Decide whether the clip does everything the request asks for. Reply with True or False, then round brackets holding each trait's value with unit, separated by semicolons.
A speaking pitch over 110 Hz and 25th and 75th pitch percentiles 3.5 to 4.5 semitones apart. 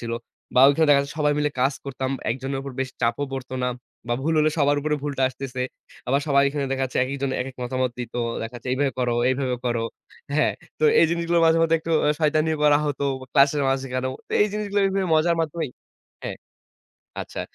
False (140 Hz; 2.9 semitones)